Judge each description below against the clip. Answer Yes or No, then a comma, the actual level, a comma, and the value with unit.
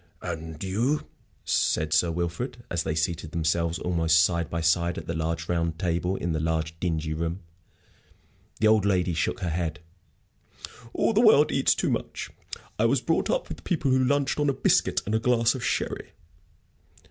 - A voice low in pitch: Yes, very low, 85 Hz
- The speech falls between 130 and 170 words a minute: No, average, 180 wpm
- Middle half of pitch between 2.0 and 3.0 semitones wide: No, average, 5.2 semitones